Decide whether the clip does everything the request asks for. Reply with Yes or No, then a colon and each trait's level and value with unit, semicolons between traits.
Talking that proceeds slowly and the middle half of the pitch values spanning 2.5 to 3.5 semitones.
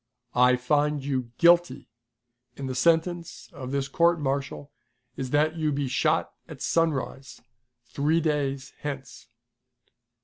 Yes: slow, 125 wpm; average, 3.0 semitones